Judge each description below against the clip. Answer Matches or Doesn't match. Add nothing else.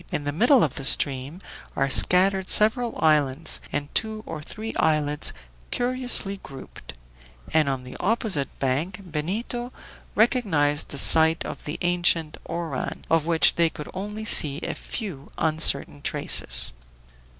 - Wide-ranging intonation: Matches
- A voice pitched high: Doesn't match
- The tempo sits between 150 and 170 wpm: Doesn't match